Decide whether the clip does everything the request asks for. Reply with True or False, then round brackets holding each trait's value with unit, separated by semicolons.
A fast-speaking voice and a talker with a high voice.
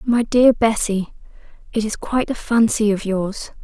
False (165 wpm; 220 Hz)